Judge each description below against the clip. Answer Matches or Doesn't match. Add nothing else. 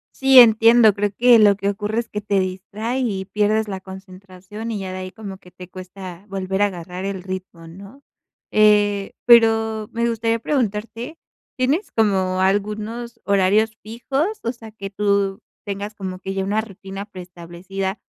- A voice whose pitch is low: Doesn't match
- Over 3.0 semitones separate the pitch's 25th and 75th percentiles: Doesn't match